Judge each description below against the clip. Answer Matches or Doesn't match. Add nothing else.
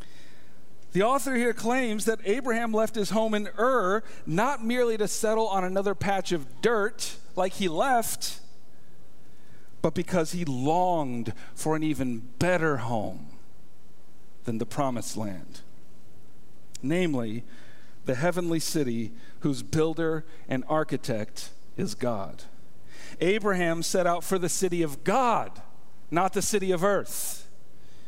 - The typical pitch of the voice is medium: Matches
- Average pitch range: Doesn't match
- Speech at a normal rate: Doesn't match